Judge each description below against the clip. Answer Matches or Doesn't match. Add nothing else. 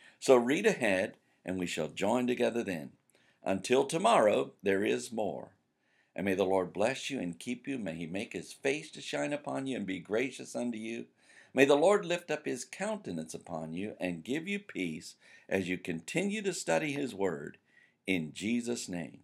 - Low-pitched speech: Matches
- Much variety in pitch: Matches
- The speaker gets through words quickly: Doesn't match